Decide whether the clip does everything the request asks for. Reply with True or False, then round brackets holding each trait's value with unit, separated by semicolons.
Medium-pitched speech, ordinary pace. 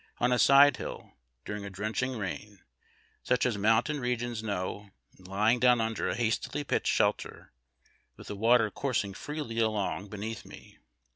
False (110 Hz; 155 wpm)